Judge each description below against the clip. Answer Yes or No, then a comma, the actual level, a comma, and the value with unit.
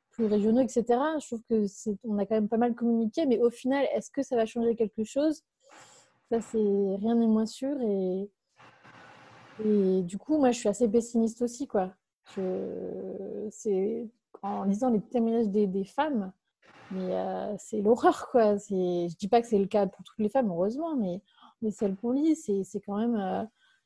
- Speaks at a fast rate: No, average, 195 wpm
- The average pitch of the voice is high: Yes, high, 220 Hz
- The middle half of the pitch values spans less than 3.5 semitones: Yes, average, 3.1 semitones